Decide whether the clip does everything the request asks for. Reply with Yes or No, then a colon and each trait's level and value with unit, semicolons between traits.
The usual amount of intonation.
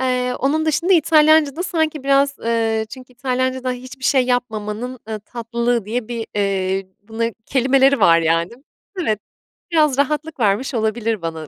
Yes: average, 4.1 semitones